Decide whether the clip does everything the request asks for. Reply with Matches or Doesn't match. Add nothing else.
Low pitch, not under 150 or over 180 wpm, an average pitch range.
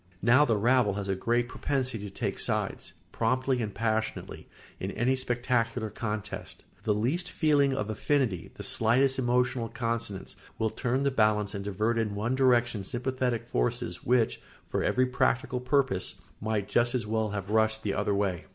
Matches